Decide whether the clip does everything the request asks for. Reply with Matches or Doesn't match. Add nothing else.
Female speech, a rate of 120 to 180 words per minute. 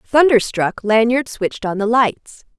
Matches